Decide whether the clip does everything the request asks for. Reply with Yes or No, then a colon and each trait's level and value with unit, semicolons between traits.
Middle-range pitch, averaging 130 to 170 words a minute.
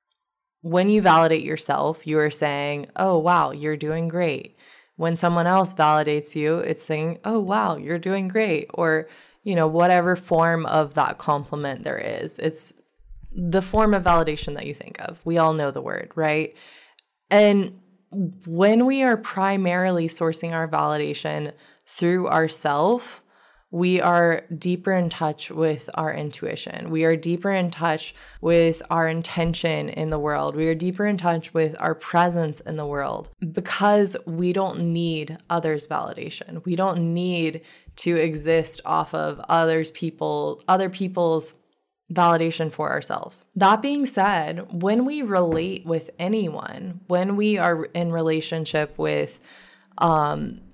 Yes: medium, 165 Hz; average, 145 wpm